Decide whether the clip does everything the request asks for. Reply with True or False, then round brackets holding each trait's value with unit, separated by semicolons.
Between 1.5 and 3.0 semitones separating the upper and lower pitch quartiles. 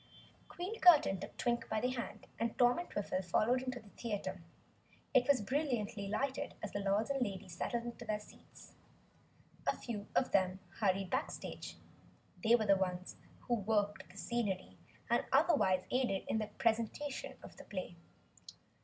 False (4.0 semitones)